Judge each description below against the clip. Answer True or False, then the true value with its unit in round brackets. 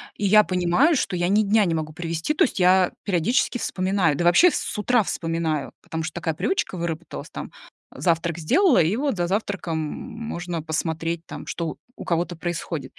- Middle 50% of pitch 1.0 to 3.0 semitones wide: False (3.7 semitones)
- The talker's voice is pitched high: False (175 Hz)